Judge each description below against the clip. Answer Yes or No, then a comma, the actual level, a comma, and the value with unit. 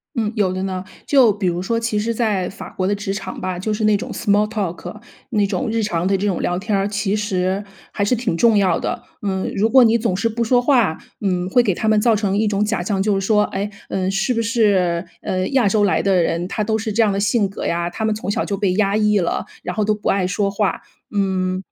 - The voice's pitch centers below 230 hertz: Yes, high, 205 Hz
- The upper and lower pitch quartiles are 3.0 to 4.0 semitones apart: No, narrow, 2.4 semitones